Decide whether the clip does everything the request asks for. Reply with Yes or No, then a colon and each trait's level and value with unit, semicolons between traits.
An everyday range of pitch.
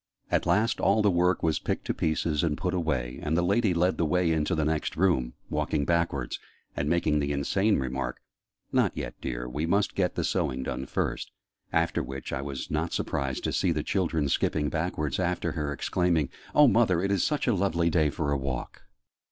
Yes: average, 4.0 semitones